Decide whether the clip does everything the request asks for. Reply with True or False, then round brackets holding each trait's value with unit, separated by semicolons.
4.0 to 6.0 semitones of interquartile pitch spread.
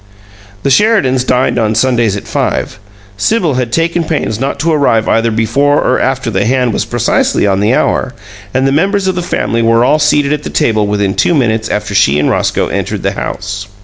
True (5.1 semitones)